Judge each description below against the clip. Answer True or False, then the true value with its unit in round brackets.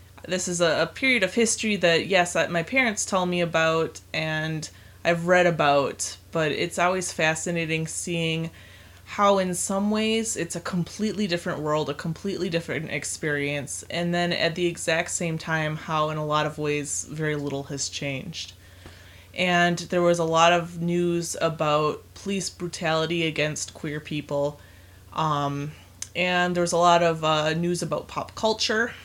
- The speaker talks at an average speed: True (160 wpm)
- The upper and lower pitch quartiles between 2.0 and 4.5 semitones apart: True (2.7 semitones)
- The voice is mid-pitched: True (165 Hz)